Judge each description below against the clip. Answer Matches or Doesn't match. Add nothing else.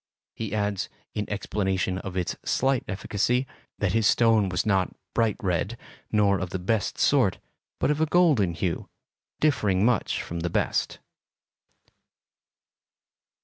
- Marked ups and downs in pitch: Doesn't match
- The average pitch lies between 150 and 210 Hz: Doesn't match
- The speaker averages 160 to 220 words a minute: Doesn't match